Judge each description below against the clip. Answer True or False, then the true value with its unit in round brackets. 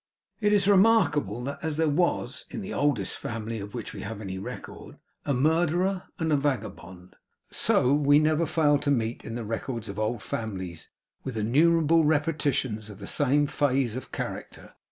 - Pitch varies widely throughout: True (6.1 semitones)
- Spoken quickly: False (175 wpm)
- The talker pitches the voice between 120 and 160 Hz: True (140 Hz)